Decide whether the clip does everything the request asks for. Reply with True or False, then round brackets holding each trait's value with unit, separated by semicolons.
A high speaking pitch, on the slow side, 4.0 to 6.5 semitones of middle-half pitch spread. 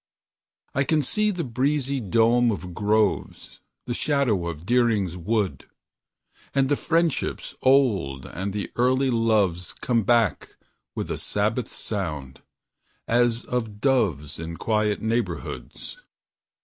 False (115 Hz; 120 wpm; 4.8 semitones)